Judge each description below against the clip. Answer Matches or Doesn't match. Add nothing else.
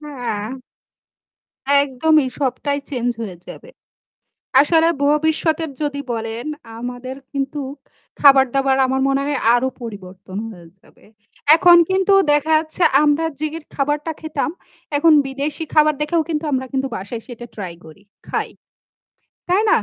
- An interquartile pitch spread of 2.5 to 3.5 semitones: Doesn't match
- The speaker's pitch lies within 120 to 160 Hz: Doesn't match